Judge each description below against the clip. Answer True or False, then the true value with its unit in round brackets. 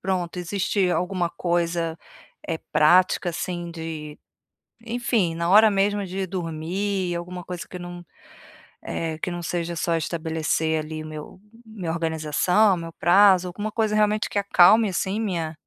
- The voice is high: False (175 Hz)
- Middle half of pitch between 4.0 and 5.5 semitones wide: False (3.0 semitones)